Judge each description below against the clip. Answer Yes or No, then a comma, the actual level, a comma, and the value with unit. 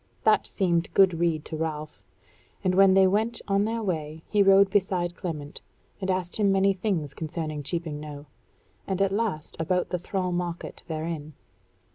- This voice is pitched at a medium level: Yes, medium, 180 Hz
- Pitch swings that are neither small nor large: Yes, average, 3.5 semitones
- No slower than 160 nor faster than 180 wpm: Yes, average, 165 wpm